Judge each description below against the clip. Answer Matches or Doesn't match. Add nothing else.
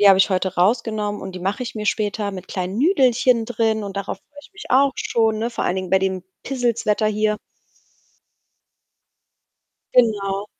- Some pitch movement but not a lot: Matches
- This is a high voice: Matches